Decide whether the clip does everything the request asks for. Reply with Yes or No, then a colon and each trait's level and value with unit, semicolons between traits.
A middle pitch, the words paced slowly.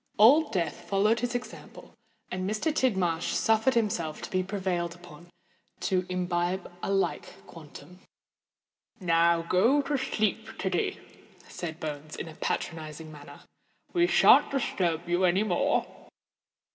Yes: medium, 180 Hz; slow, 130 wpm